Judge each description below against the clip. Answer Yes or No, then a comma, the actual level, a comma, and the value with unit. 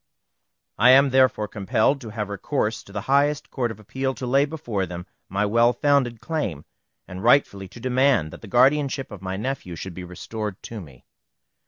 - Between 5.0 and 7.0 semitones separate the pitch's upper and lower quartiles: Yes, average, 5.3 semitones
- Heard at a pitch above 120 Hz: No, low, 115 Hz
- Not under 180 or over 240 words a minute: Yes, average, 185 wpm